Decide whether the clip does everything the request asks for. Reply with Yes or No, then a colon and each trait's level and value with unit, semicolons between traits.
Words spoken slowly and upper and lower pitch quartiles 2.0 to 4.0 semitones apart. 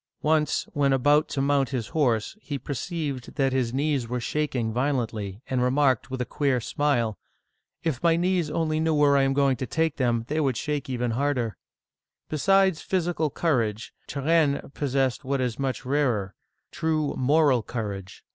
No: average, 165 wpm; average, 3.5 semitones